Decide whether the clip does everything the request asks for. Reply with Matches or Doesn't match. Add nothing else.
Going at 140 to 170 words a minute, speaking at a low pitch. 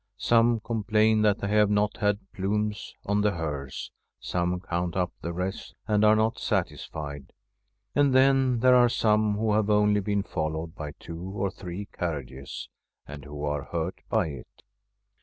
Matches